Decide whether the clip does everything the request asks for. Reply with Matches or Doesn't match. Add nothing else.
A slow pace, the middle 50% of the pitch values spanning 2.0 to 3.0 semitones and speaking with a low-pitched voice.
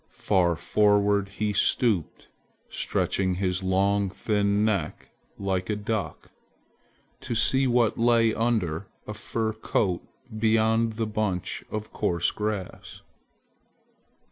Matches